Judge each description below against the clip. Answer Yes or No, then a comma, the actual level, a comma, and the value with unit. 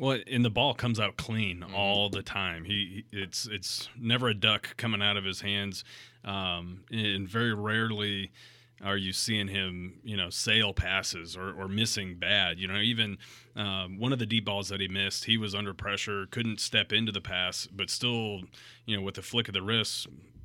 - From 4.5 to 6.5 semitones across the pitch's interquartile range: No, average, 2.7 semitones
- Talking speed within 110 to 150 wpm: No, average, 200 wpm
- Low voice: Yes, low, 100 Hz